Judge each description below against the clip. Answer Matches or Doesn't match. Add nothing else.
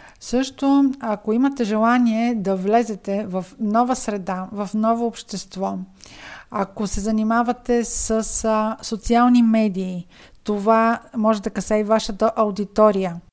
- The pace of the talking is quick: Doesn't match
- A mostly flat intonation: Matches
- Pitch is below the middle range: Doesn't match